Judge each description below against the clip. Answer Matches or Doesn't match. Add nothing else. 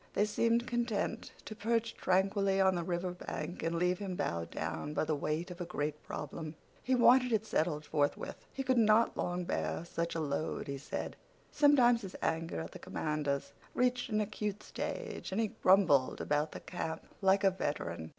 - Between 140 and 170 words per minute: Doesn't match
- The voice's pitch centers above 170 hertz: Matches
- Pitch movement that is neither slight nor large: Doesn't match